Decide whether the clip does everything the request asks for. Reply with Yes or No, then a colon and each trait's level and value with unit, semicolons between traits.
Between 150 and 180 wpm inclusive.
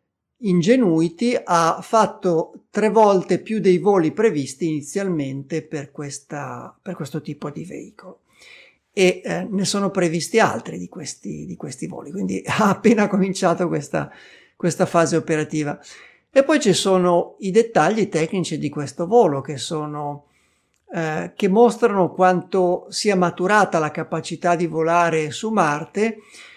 No: average, 135 wpm